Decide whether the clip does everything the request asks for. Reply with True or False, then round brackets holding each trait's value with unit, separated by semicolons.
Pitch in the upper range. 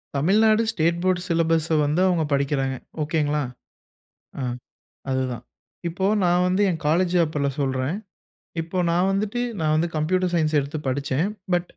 False (165 Hz)